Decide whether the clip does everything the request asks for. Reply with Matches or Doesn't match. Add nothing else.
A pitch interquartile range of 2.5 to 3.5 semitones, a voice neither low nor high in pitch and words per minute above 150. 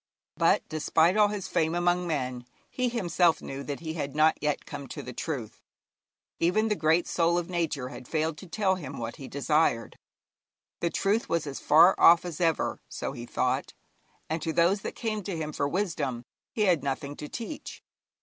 Doesn't match